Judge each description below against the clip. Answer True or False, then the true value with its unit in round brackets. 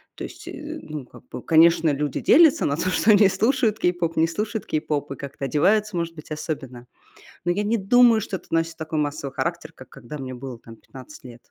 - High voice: False (165 Hz)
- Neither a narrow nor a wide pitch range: False (6.3 semitones)